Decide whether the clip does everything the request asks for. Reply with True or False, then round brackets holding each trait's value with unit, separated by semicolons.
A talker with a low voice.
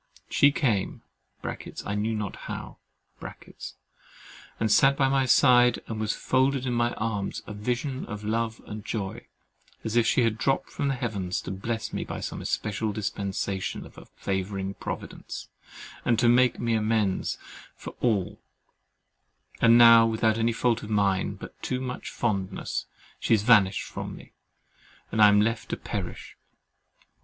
True (110 Hz)